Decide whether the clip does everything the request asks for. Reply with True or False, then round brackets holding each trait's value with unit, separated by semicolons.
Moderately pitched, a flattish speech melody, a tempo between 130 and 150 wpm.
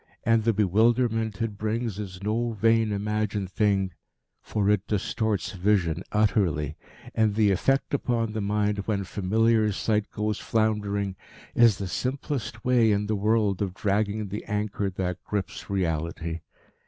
False (105 Hz; 2.1 semitones; 140 wpm)